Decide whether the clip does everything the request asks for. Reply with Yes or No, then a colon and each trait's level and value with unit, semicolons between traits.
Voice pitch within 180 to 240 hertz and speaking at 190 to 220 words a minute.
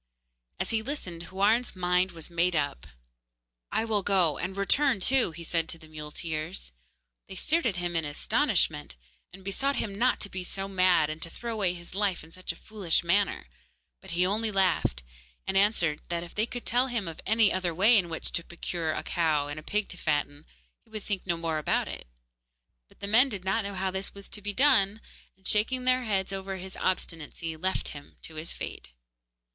Yes: medium, 185 Hz; fast, 205 wpm